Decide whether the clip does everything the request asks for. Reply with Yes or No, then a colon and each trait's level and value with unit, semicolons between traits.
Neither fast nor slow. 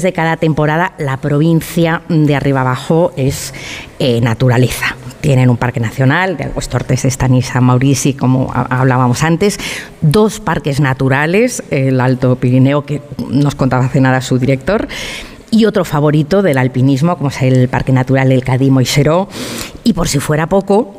Yes: average, 155 wpm